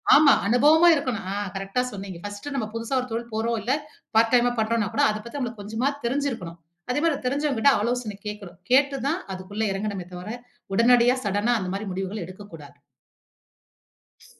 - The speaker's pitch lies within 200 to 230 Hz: Yes, high, 225 Hz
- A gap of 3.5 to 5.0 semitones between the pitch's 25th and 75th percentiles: Yes, average, 4.0 semitones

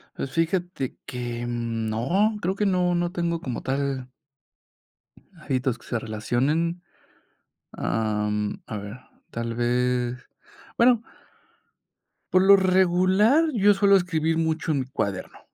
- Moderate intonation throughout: No, wide, 7.2 semitones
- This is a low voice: No, medium, 145 Hz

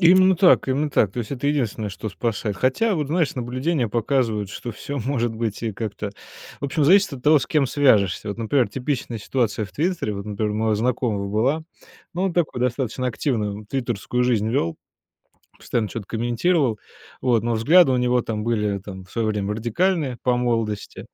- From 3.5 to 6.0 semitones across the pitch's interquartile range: Yes, average, 4.5 semitones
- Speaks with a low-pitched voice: Yes, low, 120 Hz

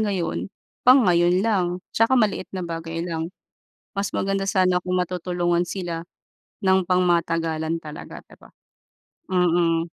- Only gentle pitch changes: Yes, narrow, 2.1 semitones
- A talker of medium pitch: Yes, medium, 175 Hz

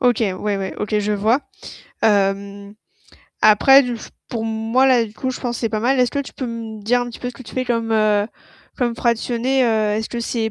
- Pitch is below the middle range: No, high, 230 Hz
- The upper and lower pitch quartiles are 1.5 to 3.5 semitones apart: Yes, narrow, 2.6 semitones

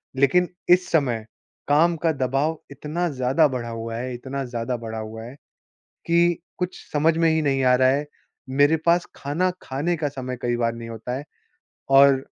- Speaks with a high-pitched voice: No, low, 135 Hz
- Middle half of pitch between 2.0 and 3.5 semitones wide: No, average, 4.6 semitones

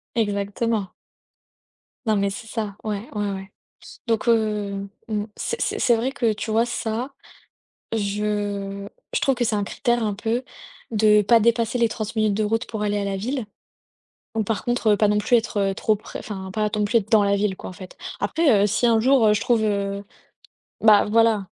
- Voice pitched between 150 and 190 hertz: No, high, 215 Hz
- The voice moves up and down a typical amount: No, narrow, 2.1 semitones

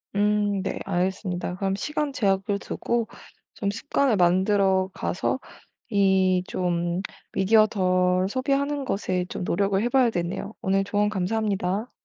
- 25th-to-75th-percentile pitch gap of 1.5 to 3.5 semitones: Yes, narrow, 2.6 semitones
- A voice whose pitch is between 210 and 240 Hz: No, high, 195 Hz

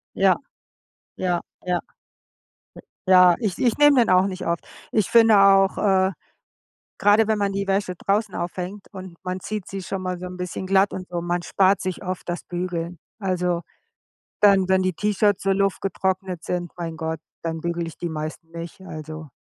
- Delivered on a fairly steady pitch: Yes, narrow, 2.0 semitones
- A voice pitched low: No, medium, 185 Hz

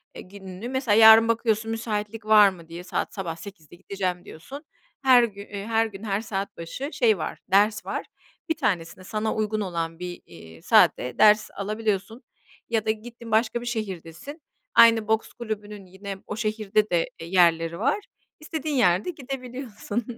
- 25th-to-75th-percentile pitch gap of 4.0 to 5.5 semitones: No, average, 3.2 semitones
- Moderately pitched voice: No, high, 210 Hz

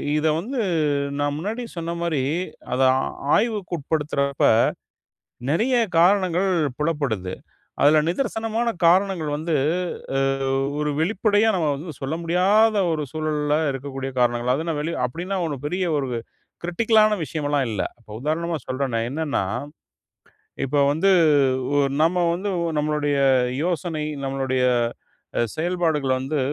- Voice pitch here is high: No, medium, 160 Hz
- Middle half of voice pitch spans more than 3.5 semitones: Yes, average, 4.1 semitones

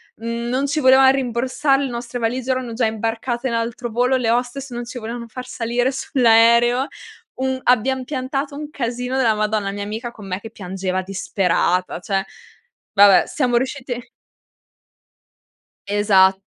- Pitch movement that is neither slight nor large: Yes, average, 3.0 semitones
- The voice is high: Yes, high, 240 Hz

